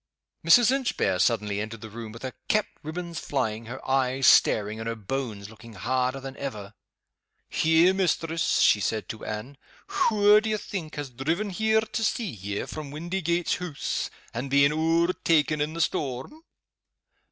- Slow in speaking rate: No, average, 165 wpm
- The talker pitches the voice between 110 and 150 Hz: Yes, medium, 140 Hz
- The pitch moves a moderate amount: No, wide, 7.0 semitones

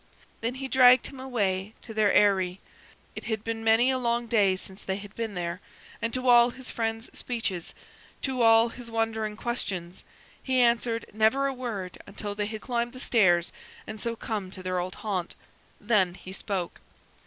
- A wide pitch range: No, average, 3.6 semitones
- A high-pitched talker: Yes, high, 225 Hz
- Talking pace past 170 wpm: Yes, average, 180 wpm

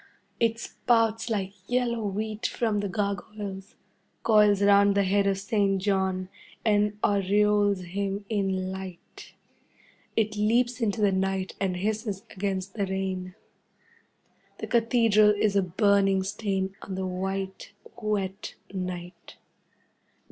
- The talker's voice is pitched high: Yes, high, 200 Hz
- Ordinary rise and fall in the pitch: No, narrow, 1.9 semitones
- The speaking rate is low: Yes, slow, 120 wpm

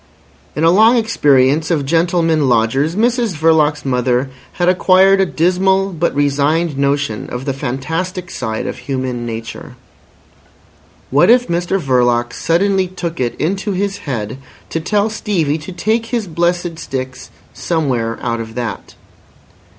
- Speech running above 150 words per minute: No, average, 140 wpm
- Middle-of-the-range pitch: Yes, medium, 160 Hz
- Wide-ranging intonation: Yes, wide, 5.9 semitones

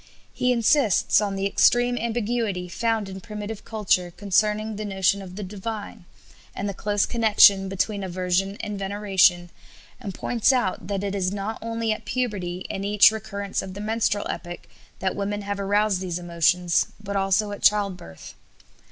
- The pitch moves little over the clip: Yes, narrow, 2.1 semitones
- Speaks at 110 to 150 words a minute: No, average, 160 wpm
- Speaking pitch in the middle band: No, high, 200 Hz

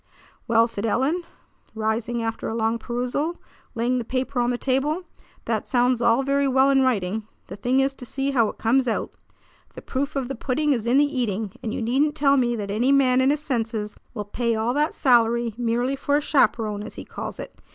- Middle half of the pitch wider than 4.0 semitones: No, average, 3.2 semitones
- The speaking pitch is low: No, high, 245 Hz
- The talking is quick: Yes, fast, 215 wpm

